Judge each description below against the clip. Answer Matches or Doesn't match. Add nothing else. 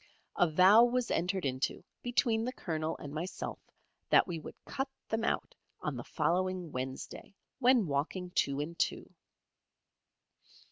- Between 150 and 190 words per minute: Doesn't match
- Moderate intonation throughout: Doesn't match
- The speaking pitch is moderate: Matches